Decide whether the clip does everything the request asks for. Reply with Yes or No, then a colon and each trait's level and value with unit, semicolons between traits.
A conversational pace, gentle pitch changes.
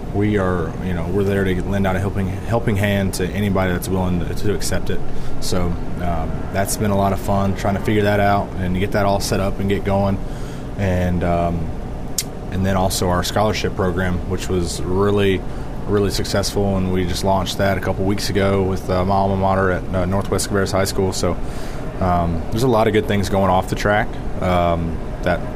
No: fast, 210 wpm; narrow, 1.7 semitones